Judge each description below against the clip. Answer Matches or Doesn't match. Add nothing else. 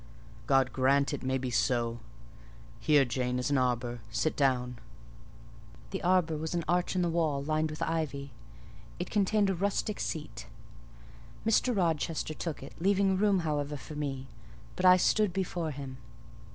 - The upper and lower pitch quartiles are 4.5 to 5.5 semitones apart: Matches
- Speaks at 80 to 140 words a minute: Doesn't match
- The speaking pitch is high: Doesn't match